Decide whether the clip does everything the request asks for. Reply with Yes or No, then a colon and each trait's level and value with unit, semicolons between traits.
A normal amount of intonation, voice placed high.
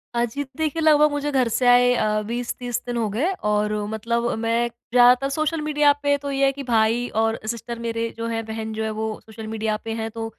Yes: average, 3.6 semitones; high, 235 Hz